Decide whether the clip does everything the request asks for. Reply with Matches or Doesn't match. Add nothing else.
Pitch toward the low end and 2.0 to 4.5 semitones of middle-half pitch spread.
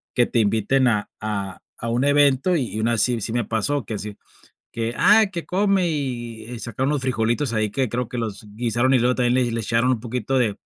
Matches